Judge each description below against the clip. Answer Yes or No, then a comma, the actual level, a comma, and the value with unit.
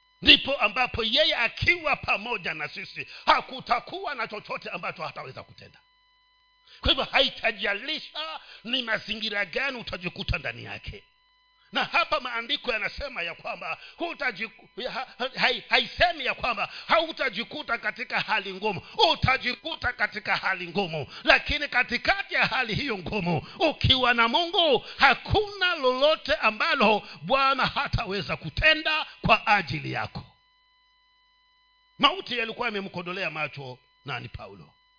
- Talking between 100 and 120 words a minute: Yes, average, 110 wpm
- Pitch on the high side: Yes, very high, 260 Hz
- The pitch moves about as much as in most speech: No, wide, 8.0 semitones